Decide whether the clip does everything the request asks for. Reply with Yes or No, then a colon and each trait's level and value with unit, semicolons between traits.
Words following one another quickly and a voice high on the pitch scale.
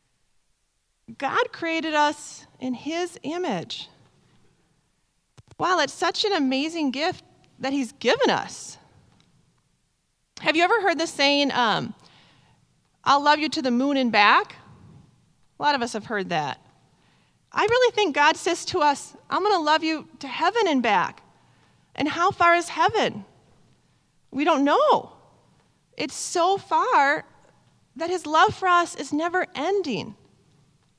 No: average, 140 wpm; very high, 320 Hz